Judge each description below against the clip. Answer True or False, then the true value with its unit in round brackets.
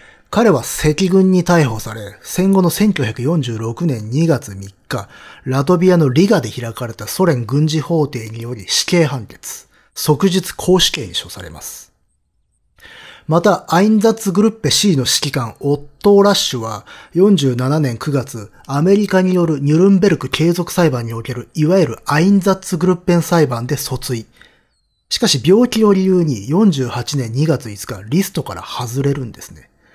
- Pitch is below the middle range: False (150 Hz)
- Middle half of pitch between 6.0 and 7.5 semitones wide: True (7.1 semitones)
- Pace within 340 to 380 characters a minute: False (290 characters per minute)